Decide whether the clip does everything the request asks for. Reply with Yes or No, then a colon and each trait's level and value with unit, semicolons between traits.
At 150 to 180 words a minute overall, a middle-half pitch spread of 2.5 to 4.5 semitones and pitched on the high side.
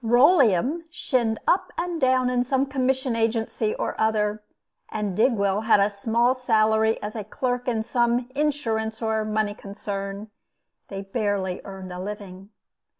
No: average, 140 wpm; average, 3.5 semitones; high, 220 Hz